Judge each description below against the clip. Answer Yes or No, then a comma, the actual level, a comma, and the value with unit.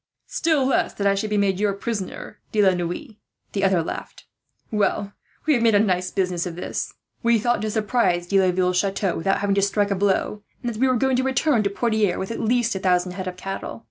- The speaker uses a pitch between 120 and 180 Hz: No, high, 200 Hz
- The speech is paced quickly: Yes, fast, 230 wpm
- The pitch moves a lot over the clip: No, average, 3.5 semitones